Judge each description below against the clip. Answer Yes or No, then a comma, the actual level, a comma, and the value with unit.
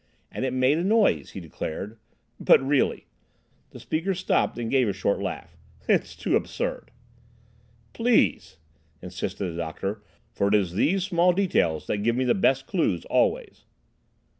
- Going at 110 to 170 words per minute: Yes, average, 140 wpm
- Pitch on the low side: Yes, low, 120 Hz